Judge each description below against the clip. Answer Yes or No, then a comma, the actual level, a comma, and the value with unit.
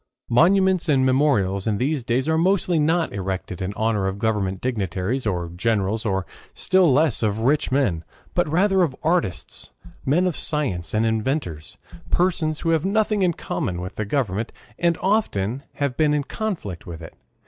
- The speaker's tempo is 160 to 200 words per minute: Yes, average, 170 wpm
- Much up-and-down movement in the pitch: Yes, wide, 8.7 semitones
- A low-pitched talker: Yes, low, 130 Hz